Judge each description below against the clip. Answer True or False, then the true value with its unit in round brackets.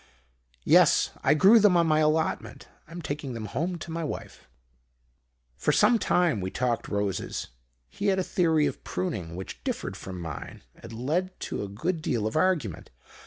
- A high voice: False (150 Hz)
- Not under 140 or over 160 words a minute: False (170 wpm)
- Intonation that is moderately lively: False (8.3 semitones)